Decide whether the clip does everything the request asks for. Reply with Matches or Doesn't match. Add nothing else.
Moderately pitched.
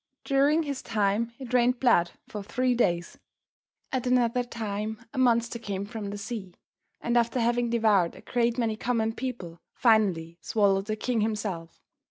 Doesn't match